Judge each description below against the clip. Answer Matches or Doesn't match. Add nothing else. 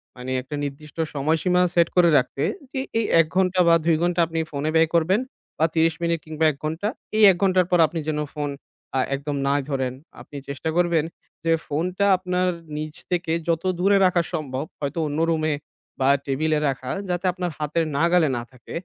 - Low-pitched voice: Doesn't match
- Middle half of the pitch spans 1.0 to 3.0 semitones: Doesn't match